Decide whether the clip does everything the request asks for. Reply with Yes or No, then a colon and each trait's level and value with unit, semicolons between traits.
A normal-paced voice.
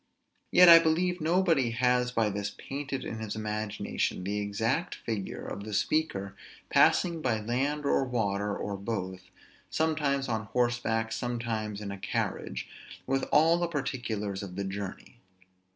Yes: average, 150 wpm